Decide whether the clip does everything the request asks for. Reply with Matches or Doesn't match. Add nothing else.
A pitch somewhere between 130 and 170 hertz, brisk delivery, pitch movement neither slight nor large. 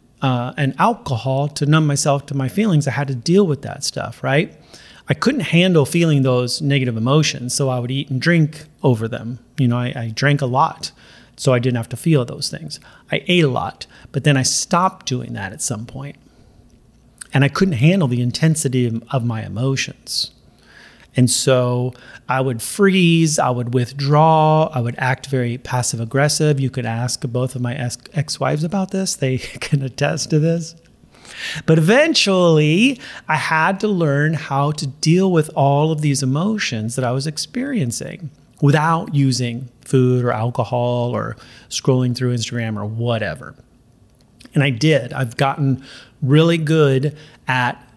Doesn't match